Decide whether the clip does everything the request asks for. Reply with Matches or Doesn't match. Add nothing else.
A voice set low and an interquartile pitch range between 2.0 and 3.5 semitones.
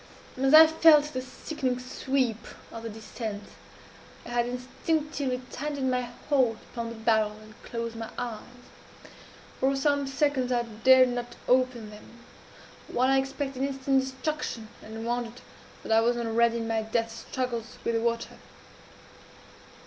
Doesn't match